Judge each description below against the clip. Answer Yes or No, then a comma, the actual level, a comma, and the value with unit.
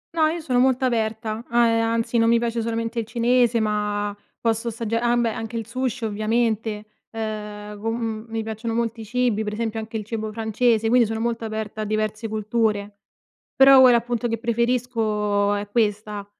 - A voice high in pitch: Yes, high, 225 Hz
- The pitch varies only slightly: Yes, narrow, 1.6 semitones